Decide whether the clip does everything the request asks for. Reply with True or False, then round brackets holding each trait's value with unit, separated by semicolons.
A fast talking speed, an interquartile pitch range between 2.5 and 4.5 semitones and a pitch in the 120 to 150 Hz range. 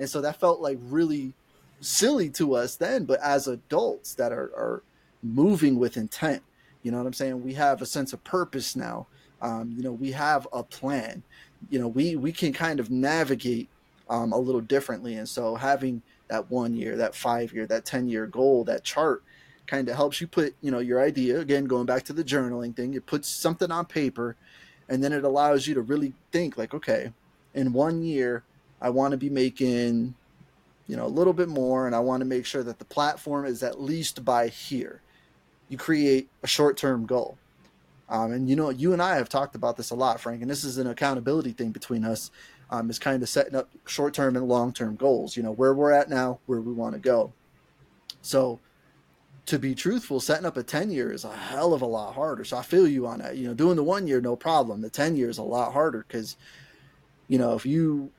True (225 wpm; 3.0 semitones; 130 Hz)